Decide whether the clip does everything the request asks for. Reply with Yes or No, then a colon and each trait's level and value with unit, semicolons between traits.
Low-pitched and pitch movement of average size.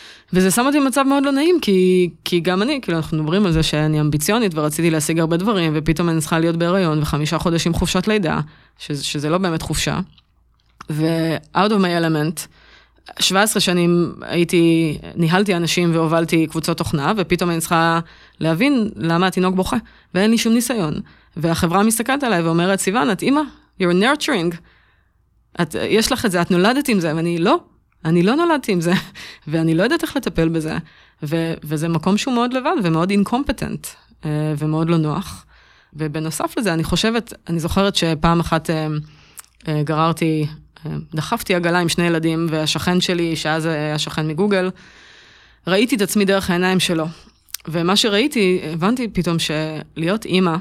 No: medium, 170 Hz; average, 3.4 semitones